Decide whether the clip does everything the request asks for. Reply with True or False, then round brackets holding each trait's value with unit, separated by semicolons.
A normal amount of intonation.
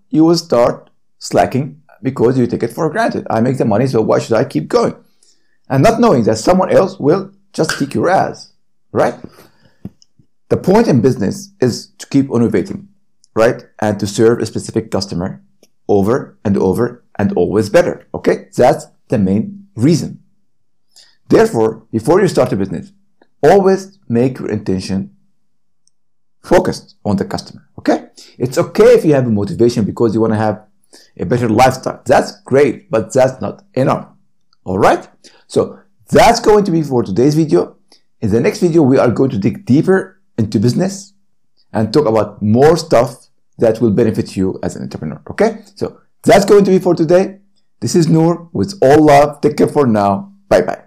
False (9.0 semitones)